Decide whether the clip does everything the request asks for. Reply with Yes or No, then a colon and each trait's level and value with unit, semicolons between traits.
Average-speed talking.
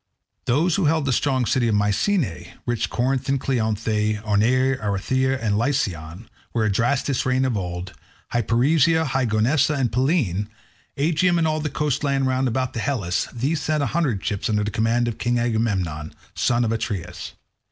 Yes: average, 165 wpm